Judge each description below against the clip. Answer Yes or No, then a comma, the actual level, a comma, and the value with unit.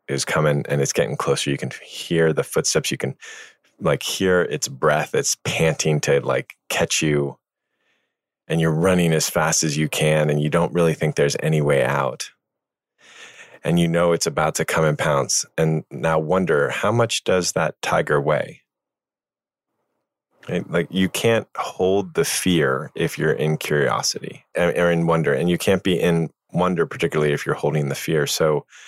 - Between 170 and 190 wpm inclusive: Yes, average, 180 wpm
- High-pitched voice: No, very low, 80 Hz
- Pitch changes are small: Yes, narrow, 2.1 semitones